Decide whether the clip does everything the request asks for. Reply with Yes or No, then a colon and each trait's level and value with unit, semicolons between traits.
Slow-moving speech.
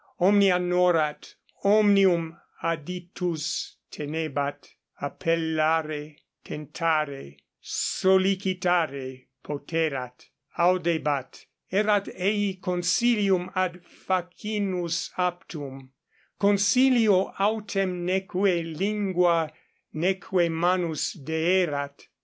Yes: slow, 60 wpm